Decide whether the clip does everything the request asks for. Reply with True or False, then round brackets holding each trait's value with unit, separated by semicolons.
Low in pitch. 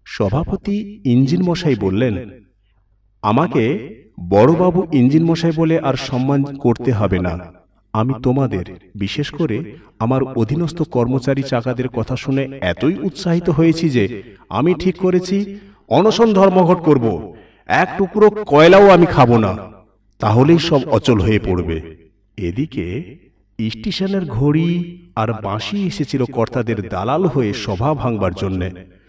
True (130 Hz)